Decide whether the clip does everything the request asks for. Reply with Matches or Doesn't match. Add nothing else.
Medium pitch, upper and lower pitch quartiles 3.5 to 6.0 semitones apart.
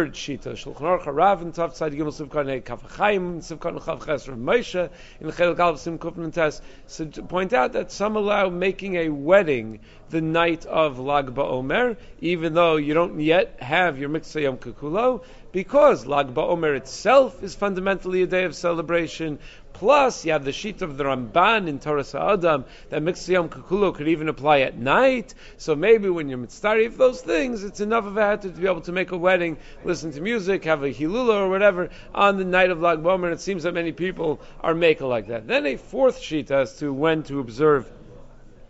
Matches